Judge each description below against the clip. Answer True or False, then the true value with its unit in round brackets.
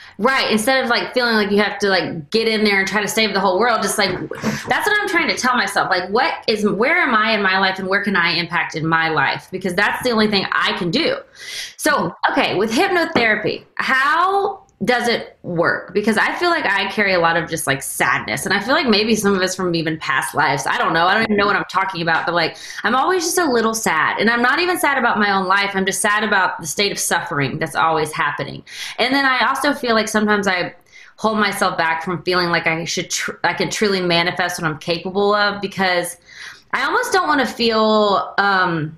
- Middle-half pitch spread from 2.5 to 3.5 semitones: False (4.3 semitones)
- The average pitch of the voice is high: True (200 Hz)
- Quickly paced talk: True (245 wpm)